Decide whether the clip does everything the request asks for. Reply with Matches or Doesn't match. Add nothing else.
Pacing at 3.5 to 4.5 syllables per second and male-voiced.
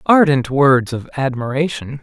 Matches